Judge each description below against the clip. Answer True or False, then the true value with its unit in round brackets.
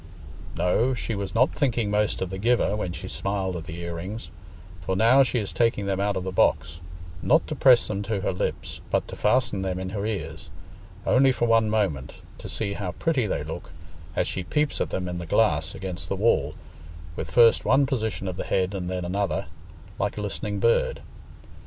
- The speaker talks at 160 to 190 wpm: False (205 wpm)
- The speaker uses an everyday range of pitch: True (3.8 semitones)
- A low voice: True (100 Hz)